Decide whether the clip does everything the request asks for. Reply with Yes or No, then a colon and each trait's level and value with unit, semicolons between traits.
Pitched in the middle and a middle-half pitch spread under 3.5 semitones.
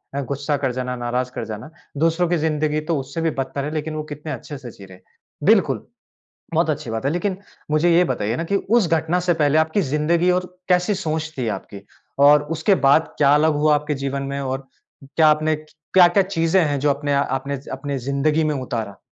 Yes: medium, 150 Hz; average, 2.9 semitones